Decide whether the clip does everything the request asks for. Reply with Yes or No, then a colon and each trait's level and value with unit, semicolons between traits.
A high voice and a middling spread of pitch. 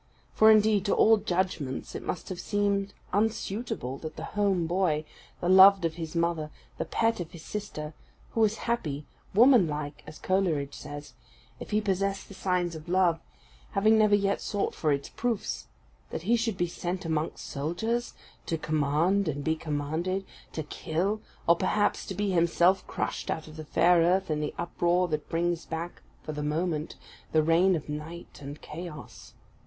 No: medium, 175 Hz; average, 4.2 semitones